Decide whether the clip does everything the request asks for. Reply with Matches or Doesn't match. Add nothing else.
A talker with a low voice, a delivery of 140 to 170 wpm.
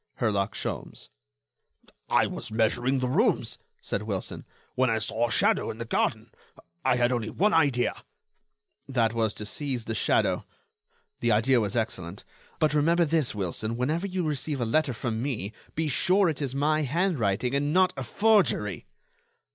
Matches